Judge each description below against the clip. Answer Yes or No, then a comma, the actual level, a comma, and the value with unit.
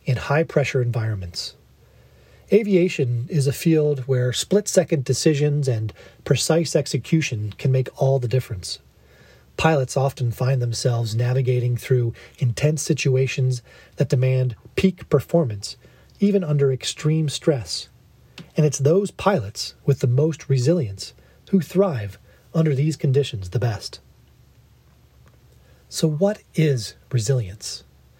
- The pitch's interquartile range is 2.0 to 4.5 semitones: No, average, 5.2 semitones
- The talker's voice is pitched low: Yes, low, 130 Hz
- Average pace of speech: No, slow, 115 wpm